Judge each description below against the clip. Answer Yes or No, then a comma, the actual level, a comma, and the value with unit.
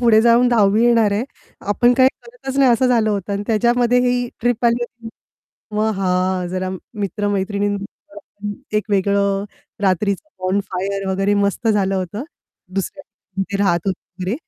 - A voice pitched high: Yes, high, 205 Hz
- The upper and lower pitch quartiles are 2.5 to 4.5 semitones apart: Yes, average, 3.3 semitones